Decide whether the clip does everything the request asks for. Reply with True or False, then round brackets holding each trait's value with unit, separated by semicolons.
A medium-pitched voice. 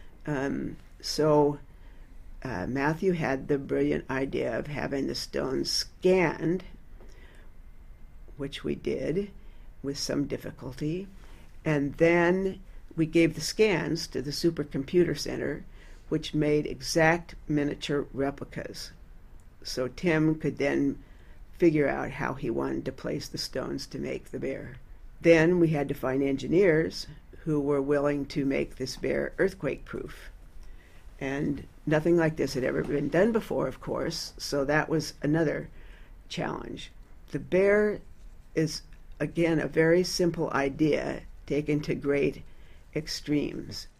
True (145 Hz)